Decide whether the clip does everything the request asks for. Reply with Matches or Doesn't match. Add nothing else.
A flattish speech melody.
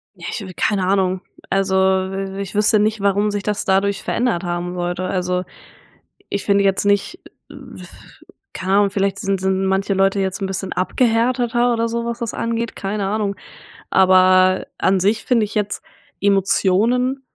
Matches